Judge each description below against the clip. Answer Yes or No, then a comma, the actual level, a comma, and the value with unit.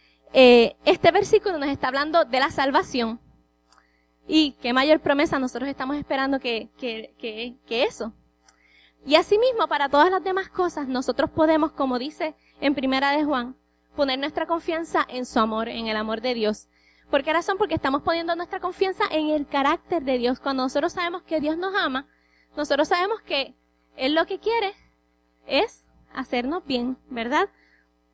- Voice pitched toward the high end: Yes, very high, 280 Hz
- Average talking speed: Yes, average, 165 wpm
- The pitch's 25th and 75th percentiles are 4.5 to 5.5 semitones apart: Yes, average, 5.2 semitones